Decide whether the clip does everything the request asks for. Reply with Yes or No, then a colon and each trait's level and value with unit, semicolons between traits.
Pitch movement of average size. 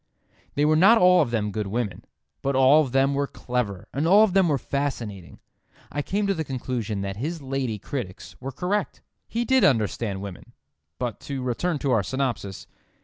No: wide, 5.8 semitones